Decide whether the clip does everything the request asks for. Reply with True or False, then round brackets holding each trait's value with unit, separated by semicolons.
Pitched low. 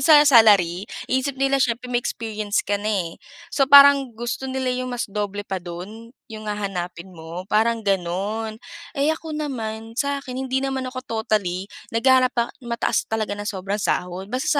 False (225 Hz)